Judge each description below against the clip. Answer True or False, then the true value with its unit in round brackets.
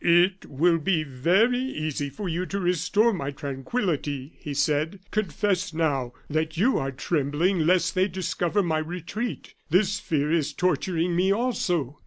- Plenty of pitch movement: False (4.3 semitones)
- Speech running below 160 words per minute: True (150 wpm)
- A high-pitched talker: False (170 Hz)